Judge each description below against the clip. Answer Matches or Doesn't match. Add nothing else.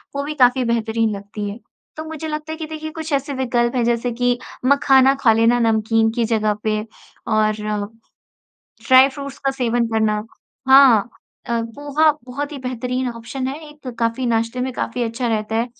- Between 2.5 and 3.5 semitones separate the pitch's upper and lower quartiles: Matches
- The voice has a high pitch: Matches